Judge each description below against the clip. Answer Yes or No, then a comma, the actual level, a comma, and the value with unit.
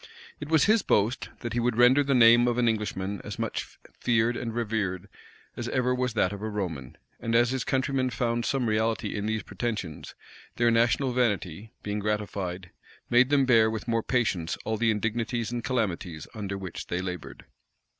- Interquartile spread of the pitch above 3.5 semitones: No, average, 3.0 semitones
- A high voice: No, low, 115 Hz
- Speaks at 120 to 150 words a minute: No, average, 185 wpm